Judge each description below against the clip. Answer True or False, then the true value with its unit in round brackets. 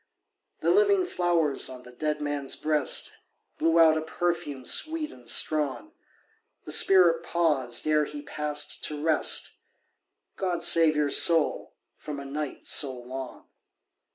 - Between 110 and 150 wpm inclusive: True (135 wpm)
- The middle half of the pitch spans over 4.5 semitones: False (3.1 semitones)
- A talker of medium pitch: True (155 Hz)